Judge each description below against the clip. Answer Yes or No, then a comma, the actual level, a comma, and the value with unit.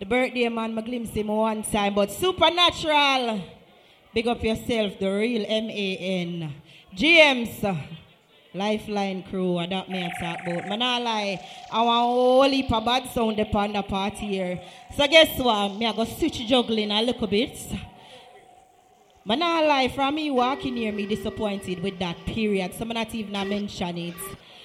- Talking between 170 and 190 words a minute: Yes, average, 180 wpm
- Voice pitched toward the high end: Yes, high, 220 Hz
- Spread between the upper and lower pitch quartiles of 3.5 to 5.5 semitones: Yes, average, 4.1 semitones